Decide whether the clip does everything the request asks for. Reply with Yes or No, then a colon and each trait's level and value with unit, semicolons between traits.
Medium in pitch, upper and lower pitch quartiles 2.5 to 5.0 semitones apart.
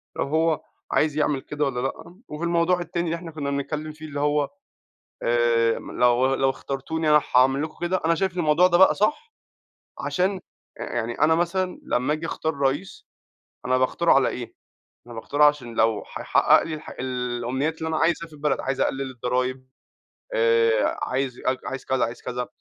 Yes: medium, 145 Hz; average, 4.2 semitones